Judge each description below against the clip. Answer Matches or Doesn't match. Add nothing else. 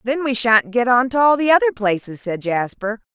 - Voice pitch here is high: Matches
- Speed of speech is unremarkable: Doesn't match